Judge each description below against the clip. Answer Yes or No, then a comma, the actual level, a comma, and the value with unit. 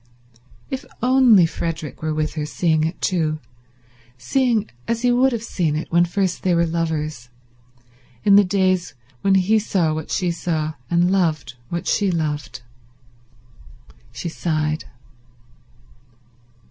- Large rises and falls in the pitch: No, average, 4.1 semitones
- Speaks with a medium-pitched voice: Yes, medium, 170 Hz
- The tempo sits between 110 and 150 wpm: Yes, slow, 135 wpm